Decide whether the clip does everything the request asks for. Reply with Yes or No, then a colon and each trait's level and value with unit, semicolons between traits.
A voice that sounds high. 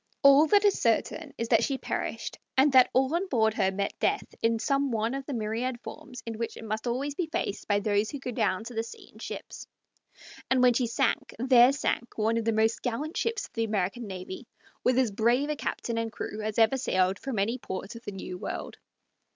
Yes: high, 230 Hz